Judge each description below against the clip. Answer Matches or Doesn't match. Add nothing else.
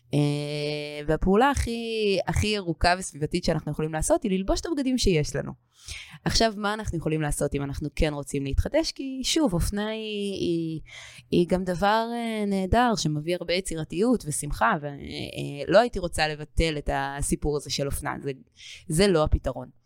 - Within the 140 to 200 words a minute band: Matches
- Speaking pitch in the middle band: Matches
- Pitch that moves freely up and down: Matches